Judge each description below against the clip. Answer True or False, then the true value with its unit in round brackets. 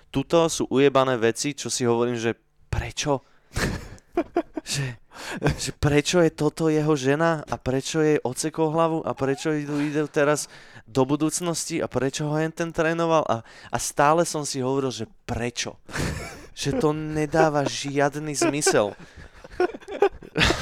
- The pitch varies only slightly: False (3.2 semitones)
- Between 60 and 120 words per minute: False (135 wpm)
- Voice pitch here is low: False (150 Hz)